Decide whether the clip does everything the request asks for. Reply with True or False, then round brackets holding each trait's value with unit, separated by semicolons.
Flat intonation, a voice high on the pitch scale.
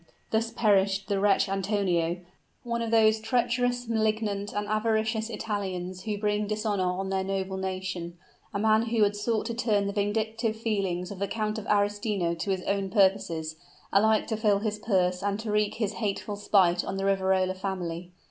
True (2.3 semitones; 205 Hz)